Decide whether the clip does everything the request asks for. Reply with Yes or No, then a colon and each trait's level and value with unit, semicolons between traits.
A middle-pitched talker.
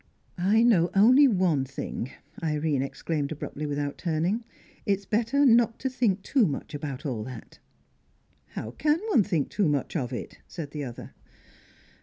Yes: medium, 165 Hz